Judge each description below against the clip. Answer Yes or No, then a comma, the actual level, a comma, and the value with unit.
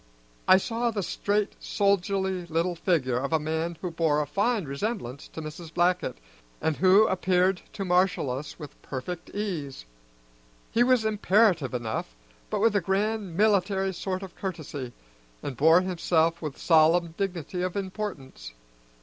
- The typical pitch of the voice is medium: Yes, medium, 180 Hz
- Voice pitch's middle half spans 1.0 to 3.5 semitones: No, average, 4.0 semitones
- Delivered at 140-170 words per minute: Yes, average, 150 wpm